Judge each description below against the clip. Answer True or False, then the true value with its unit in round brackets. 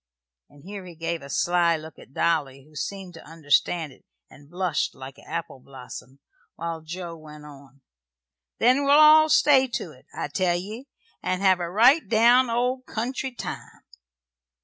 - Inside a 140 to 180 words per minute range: True (170 wpm)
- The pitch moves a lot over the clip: True (7.4 semitones)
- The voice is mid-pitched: True (175 Hz)